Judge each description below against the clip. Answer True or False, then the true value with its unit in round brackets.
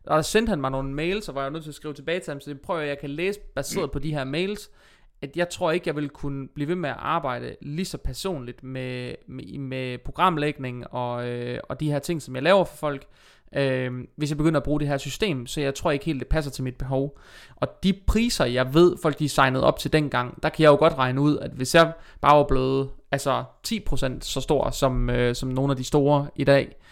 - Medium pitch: True (145 Hz)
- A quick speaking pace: True (255 wpm)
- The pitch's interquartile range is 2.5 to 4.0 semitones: True (3.1 semitones)